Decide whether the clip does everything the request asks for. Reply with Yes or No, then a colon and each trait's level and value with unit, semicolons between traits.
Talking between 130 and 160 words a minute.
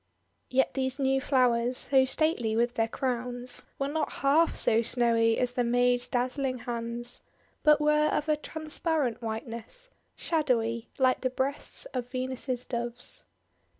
Yes: average, 150 wpm